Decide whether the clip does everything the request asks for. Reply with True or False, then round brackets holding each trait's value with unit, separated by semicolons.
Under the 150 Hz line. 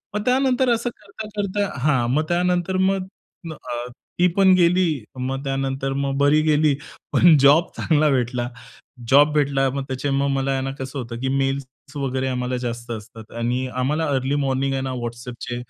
True (135 Hz)